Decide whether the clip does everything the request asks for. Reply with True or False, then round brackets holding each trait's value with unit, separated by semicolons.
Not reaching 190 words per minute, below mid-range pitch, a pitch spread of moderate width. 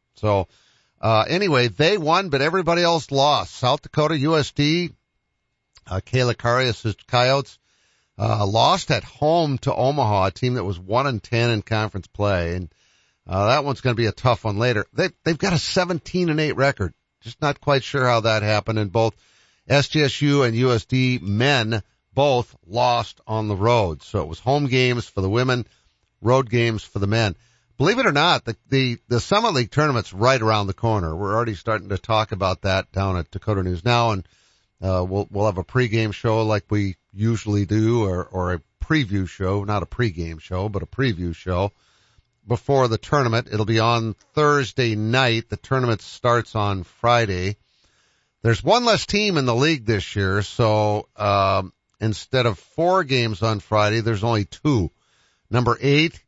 True (180 wpm; 115 Hz; 4.5 semitones)